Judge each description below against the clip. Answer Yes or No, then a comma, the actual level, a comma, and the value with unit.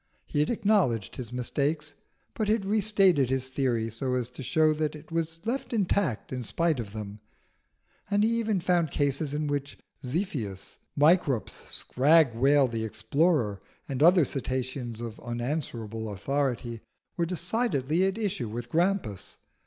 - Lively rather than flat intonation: Yes, wide, 6.5 semitones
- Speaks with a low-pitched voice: No, medium, 145 Hz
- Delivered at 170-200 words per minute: No, average, 150 wpm